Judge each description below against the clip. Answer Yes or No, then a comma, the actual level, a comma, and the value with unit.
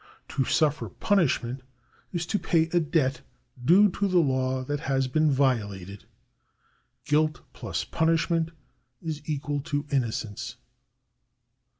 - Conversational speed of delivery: No, slow, 115 wpm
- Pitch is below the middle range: No, medium, 145 Hz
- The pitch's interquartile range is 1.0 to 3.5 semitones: No, average, 3.9 semitones